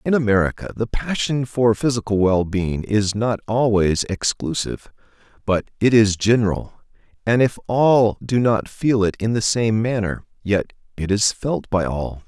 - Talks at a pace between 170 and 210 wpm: No, average, 155 wpm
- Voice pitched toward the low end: Yes, low, 110 Hz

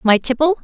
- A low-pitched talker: No, very high, 270 Hz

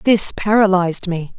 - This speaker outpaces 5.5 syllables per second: No, 5.0 syllables/s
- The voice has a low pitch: No, high, 190 Hz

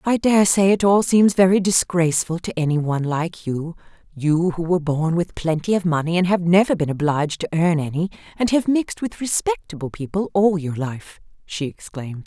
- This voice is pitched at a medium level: Yes, medium, 175 Hz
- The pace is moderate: Yes, average, 190 wpm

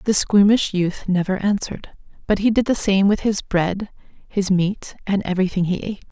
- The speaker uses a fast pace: No, average, 185 wpm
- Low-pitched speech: No, high, 195 Hz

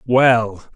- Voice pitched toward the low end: Yes, low, 115 Hz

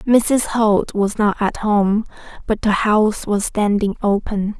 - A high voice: Yes, high, 210 Hz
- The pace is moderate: Yes, average, 155 wpm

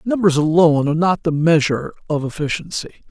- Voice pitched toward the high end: No, medium, 160 Hz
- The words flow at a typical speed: Yes, average, 155 wpm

